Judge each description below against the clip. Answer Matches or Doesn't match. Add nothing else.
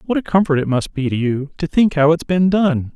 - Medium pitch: Matches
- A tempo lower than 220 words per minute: Doesn't match